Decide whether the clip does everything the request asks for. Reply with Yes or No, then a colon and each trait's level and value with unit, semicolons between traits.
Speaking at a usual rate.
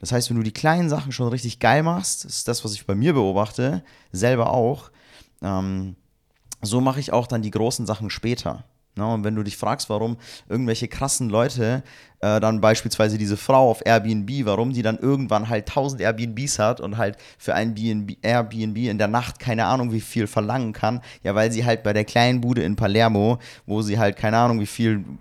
No: fast, 205 wpm